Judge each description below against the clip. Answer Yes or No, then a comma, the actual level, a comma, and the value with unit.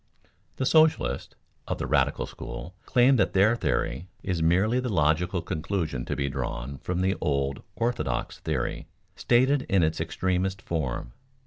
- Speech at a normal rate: Yes, average, 150 wpm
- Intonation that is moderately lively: No, wide, 6.3 semitones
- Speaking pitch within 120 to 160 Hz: No, very low, 90 Hz